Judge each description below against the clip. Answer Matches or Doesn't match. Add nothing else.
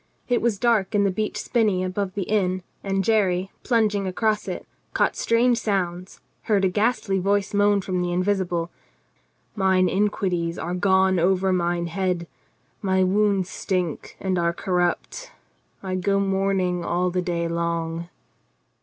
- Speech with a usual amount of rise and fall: Doesn't match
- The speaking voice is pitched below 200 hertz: Matches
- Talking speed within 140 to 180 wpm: Matches